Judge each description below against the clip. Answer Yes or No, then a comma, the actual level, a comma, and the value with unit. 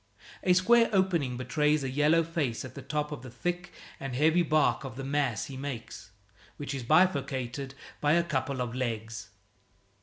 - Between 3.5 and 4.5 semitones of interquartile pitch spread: Yes, average, 3.8 semitones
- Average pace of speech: Yes, average, 175 wpm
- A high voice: No, medium, 140 Hz